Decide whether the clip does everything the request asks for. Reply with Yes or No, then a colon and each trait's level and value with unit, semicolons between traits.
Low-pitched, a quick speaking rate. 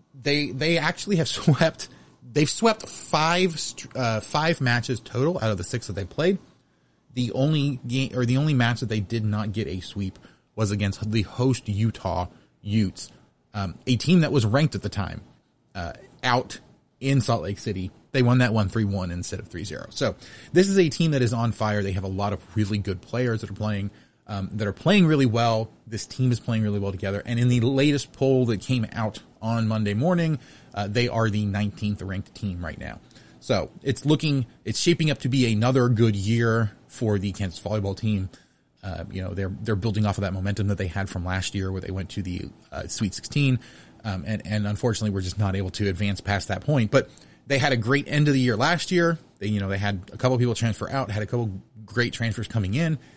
Yes: low, 110 Hz; fast, 225 wpm